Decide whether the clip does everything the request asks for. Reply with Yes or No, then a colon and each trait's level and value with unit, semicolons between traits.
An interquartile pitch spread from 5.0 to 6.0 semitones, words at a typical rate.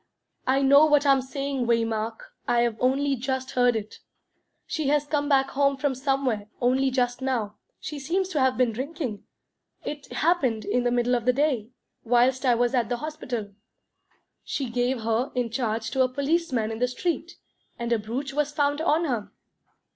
No: average, 3.0 semitones; average, 175 wpm